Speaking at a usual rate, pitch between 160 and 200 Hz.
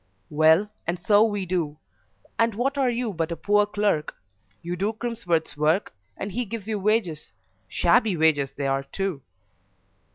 Yes: average, 160 wpm; high, 190 Hz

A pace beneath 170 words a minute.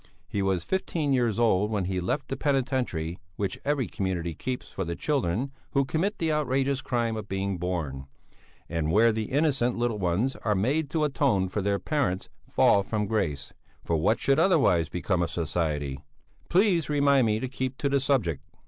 No: average, 180 wpm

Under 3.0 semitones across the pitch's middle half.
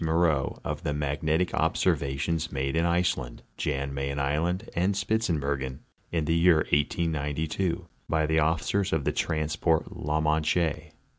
Yes: narrow, 2.6 semitones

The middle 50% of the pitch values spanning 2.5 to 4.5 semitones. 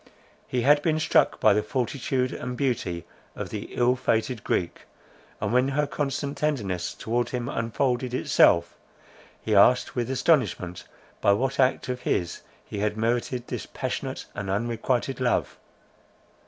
Yes: average, 3.8 semitones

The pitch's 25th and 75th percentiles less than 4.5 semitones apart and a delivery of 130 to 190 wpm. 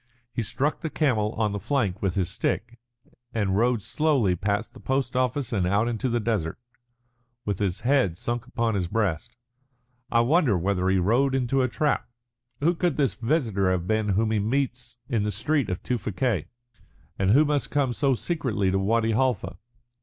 No: average, 4.8 semitones; average, 180 wpm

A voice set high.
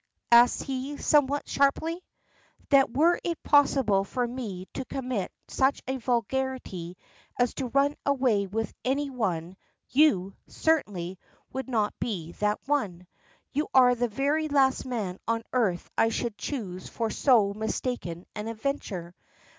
Yes: high, 245 Hz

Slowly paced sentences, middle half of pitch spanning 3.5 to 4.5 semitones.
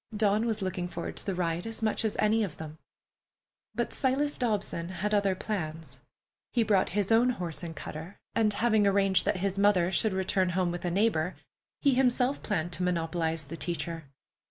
No: average, 185 wpm; average, 4.1 semitones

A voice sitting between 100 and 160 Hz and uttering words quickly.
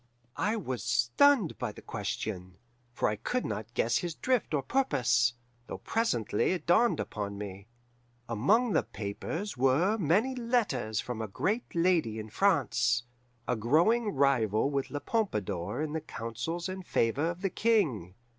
No: low, 135 Hz; average, 155 wpm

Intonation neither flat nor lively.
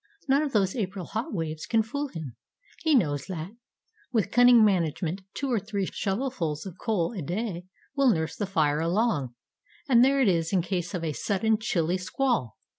No: wide, 5.9 semitones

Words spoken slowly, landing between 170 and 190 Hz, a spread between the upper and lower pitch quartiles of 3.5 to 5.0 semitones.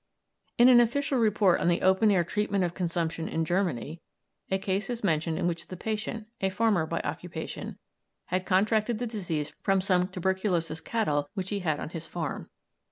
No: average, 180 wpm; medium, 185 Hz; average, 4.0 semitones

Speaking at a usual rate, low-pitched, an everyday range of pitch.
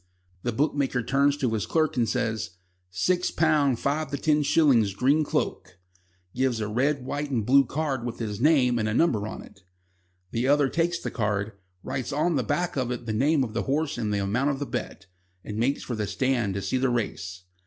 No: fast, 210 wpm; low, 130 Hz; average, 4.6 semitones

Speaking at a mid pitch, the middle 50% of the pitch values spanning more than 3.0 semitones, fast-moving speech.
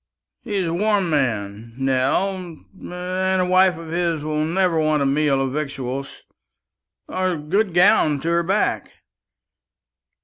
No: medium, 165 Hz; average, 4.7 semitones; average, 140 wpm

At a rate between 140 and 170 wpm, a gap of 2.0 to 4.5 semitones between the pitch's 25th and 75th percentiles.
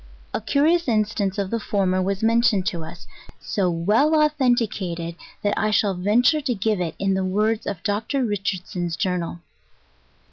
Yes: average, 155 wpm; average, 3.7 semitones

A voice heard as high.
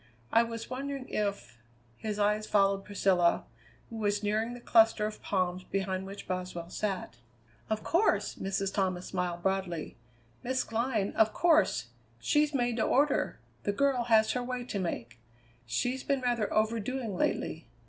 Yes: high, 210 Hz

